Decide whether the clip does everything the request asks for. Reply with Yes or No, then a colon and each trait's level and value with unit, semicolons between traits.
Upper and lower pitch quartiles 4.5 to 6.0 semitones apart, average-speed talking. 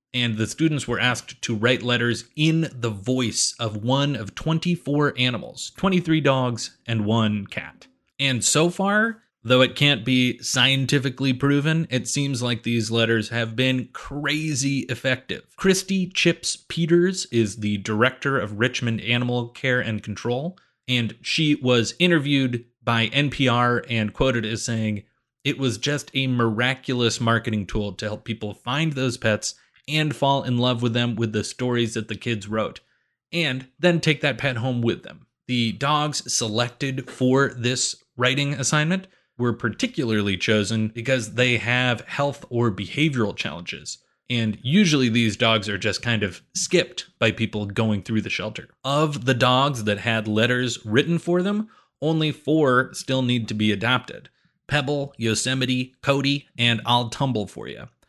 No: average, 3.7 semitones; average, 155 wpm